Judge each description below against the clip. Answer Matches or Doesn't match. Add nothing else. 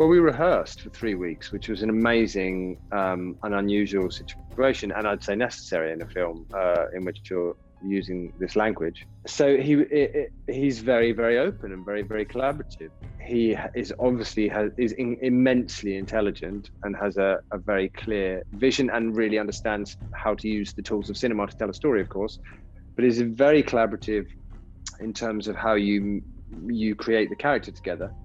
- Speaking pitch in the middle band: Doesn't match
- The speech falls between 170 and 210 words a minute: Matches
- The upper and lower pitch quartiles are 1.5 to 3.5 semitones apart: Matches